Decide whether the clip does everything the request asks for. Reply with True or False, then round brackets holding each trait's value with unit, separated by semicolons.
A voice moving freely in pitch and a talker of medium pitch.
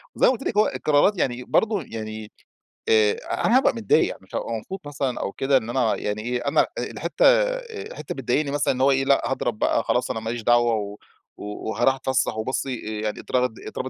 False (6.2 semitones; 130 Hz)